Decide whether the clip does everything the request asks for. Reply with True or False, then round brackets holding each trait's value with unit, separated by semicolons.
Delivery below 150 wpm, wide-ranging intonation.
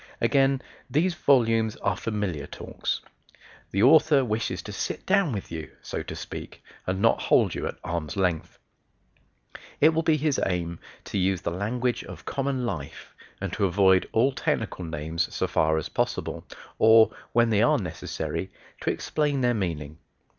False (160 wpm; 7.1 semitones)